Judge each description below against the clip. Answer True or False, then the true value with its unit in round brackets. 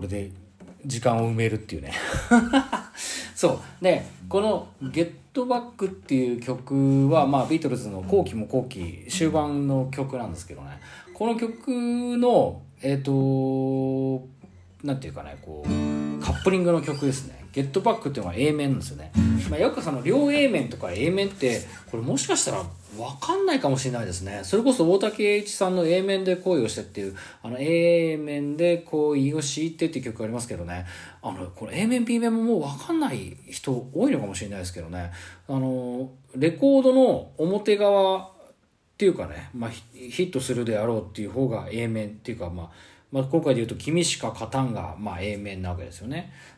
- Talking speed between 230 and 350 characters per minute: True (340 characters per minute)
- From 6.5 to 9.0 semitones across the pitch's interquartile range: True (8.6 semitones)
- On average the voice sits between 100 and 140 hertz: True (135 Hz)